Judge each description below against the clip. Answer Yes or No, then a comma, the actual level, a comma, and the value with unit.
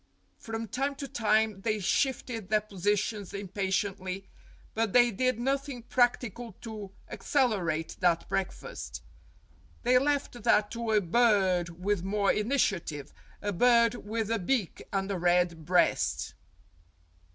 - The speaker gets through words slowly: Yes, slow, 130 wpm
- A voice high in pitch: Yes, high, 210 Hz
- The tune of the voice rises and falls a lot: No, average, 4.1 semitones